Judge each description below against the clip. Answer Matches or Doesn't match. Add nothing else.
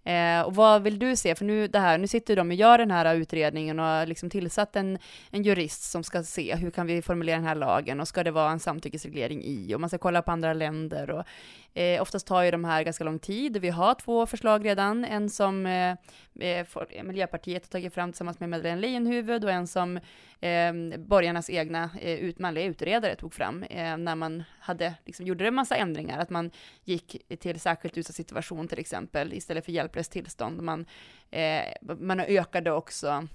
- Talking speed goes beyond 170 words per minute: Matches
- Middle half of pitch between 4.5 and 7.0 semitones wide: Doesn't match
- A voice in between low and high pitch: Matches